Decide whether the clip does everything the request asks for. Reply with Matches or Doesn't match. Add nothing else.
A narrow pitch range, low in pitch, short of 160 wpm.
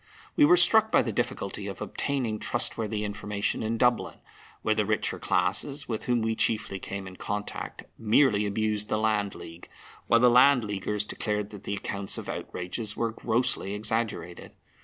Doesn't match